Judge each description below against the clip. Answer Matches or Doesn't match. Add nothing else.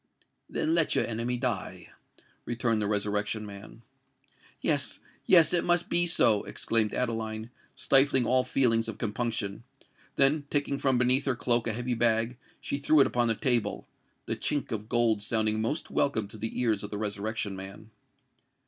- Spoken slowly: Doesn't match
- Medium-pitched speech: Doesn't match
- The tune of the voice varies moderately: Matches